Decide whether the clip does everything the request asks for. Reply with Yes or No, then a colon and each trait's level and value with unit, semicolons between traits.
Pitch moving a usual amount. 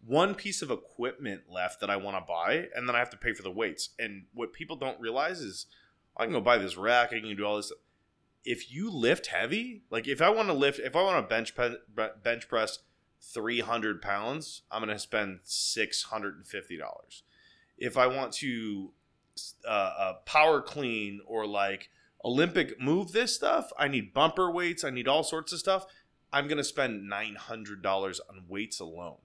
No: wide, 6.3 semitones